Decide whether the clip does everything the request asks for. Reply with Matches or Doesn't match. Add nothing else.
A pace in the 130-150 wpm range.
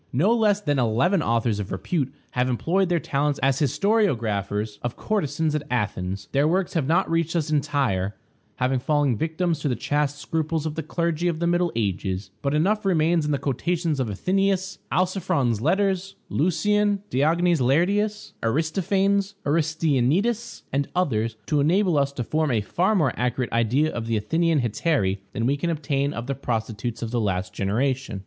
Doesn't match